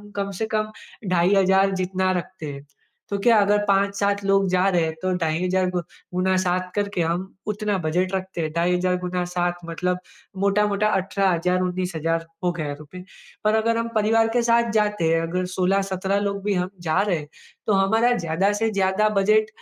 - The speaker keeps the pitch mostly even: Yes, narrow, 2.2 semitones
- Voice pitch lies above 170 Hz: Yes, high, 190 Hz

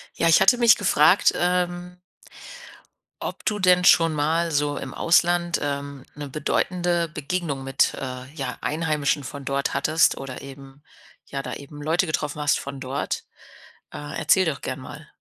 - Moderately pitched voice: Yes, medium, 150 Hz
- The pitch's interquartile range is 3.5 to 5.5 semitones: Yes, average, 3.8 semitones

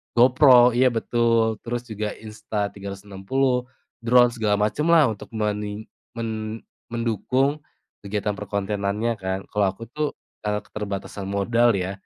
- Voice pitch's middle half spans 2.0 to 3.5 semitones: Yes, average, 2.9 semitones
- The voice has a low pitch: Yes, low, 110 Hz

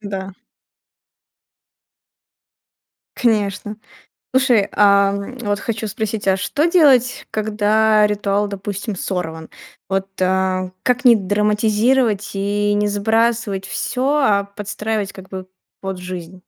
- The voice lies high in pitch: Yes, high, 205 Hz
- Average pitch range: No, narrow, 2.2 semitones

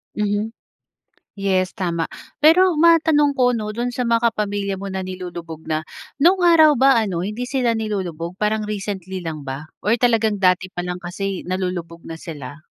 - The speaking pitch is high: Yes, high, 200 Hz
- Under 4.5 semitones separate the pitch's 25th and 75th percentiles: No, average, 4.9 semitones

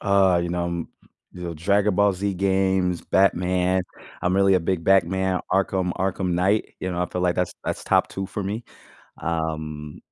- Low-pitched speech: Yes, very low, 90 Hz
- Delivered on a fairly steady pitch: Yes, narrow, 1.8 semitones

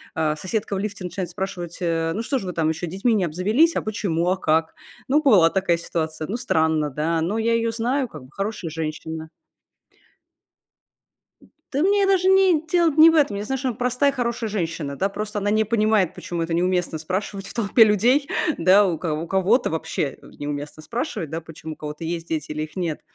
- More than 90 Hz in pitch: Yes, high, 190 Hz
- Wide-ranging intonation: Yes, wide, 6.0 semitones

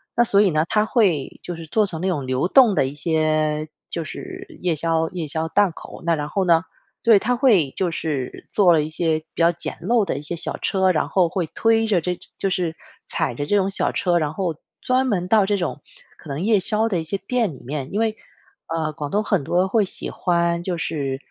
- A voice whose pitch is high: No, medium, 175 Hz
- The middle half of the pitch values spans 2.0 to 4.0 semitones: No, average, 4.6 semitones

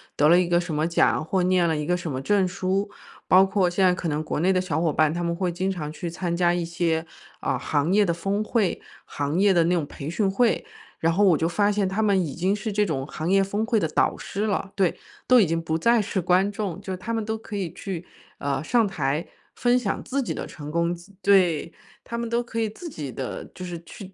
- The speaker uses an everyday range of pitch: Yes, average, 3.6 semitones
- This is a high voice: No, medium, 180 Hz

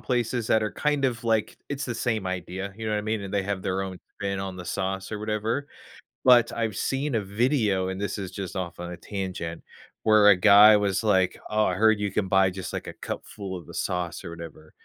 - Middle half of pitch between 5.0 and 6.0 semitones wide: No, average, 2.9 semitones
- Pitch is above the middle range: No, low, 100 Hz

